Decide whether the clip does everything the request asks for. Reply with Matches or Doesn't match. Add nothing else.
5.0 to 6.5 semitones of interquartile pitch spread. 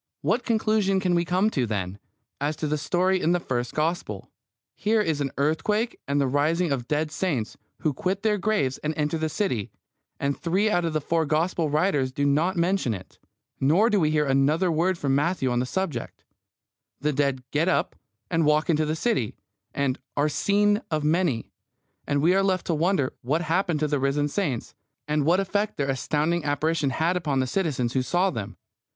Doesn't match